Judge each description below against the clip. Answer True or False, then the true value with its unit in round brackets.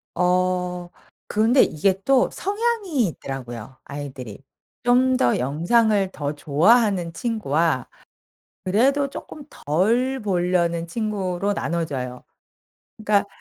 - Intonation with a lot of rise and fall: True (7.2 semitones)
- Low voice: False (185 Hz)